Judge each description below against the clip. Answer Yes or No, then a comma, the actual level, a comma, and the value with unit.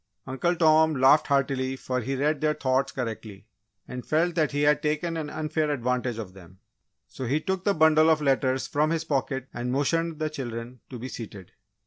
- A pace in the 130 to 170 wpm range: No, average, 190 wpm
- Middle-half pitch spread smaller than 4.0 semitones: Yes, average, 3.5 semitones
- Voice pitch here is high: No, medium, 140 Hz